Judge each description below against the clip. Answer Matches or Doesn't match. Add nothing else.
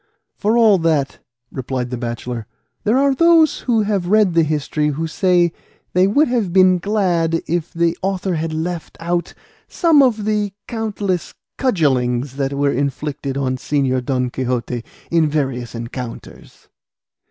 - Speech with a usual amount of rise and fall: Doesn't match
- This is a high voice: Doesn't match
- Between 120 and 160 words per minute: Matches